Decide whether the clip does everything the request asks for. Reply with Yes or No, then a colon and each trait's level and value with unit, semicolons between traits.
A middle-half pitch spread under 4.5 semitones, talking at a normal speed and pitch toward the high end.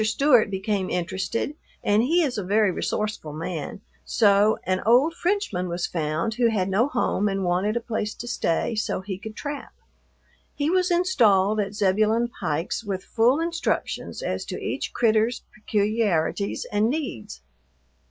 Yes: average, 4.0 semitones; average, 150 wpm; high, 215 Hz